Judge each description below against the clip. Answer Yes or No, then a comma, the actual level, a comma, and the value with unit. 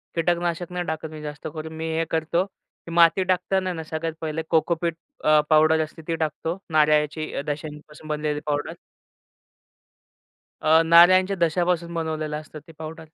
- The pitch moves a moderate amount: No, narrow, 1.7 semitones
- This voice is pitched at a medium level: Yes, medium, 160 Hz